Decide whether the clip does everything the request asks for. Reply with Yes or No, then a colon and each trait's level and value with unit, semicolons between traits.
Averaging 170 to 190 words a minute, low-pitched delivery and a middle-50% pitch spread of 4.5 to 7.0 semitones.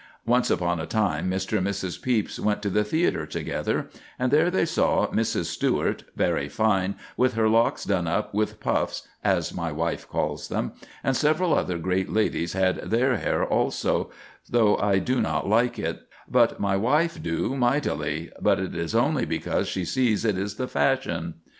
Yes: average, 180 wpm; low, 105 Hz; average, 5.2 semitones